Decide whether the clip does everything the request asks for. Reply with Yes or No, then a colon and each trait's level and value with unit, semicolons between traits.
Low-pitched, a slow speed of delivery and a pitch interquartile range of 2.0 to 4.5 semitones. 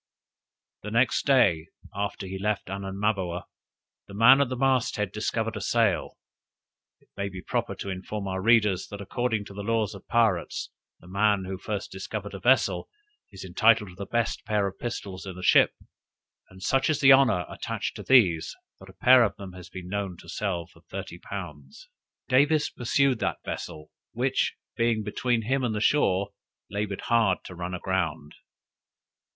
No: low, 100 Hz; average, 175 wpm; average, 3.7 semitones